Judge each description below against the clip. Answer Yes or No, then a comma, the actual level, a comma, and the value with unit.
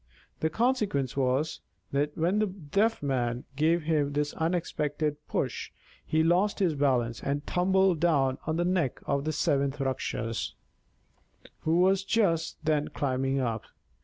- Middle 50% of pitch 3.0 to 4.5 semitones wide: Yes, average, 4.1 semitones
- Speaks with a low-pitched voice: No, medium, 150 Hz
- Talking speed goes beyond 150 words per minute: No, average, 145 wpm